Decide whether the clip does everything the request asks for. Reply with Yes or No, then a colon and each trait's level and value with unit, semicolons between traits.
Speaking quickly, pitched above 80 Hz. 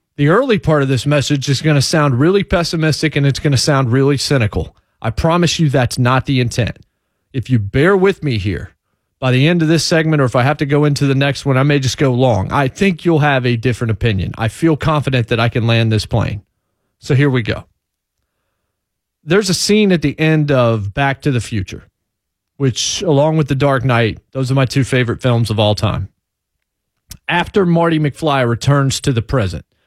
Yes: fast, 215 wpm; low, 135 Hz